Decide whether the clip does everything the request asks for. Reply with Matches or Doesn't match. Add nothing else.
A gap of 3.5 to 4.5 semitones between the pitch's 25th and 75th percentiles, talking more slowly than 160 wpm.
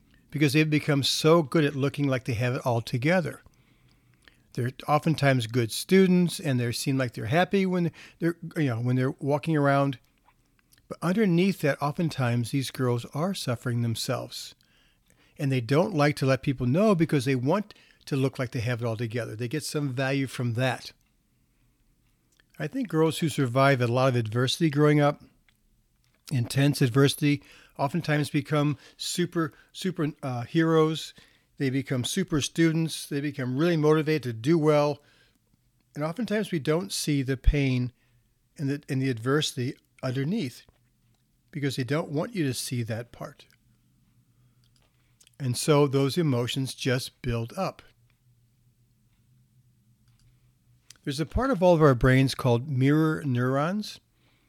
Matches